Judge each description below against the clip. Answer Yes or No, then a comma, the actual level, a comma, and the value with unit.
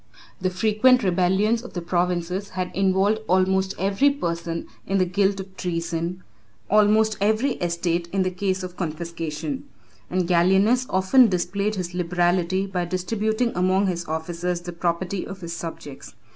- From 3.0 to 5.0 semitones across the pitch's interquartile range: No, narrow, 2.4 semitones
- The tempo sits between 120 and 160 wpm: Yes, average, 145 wpm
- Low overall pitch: No, medium, 185 Hz